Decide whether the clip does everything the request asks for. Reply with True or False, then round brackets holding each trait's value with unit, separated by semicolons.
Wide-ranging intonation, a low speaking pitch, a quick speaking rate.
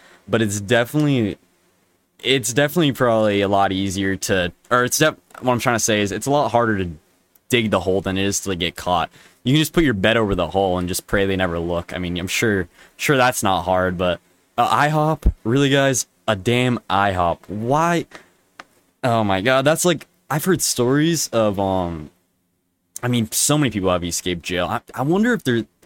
True (6.0 semitones; 110 Hz; 215 wpm)